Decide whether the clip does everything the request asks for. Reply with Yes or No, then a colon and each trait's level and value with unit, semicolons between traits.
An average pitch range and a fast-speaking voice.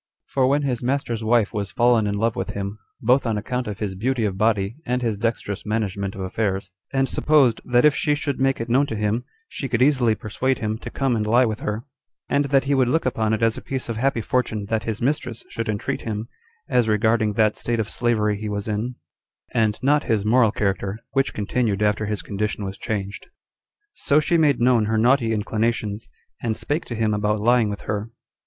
Yes: average, 3.0 semitones; fast, 215 wpm